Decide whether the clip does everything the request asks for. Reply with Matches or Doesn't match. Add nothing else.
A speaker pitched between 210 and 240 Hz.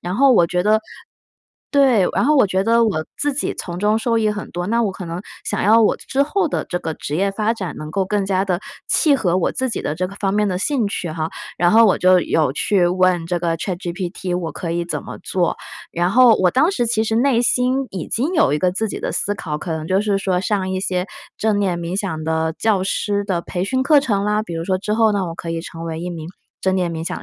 Doesn't match